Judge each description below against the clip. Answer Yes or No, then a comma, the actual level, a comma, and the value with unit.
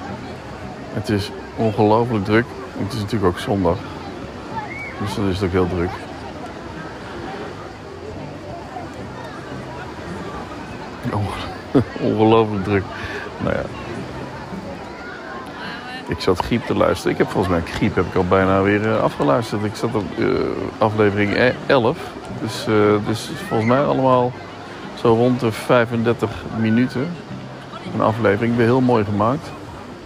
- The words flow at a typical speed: No, slow, 115 wpm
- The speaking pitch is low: Yes, low, 105 Hz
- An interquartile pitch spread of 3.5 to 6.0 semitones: No, average, 3.0 semitones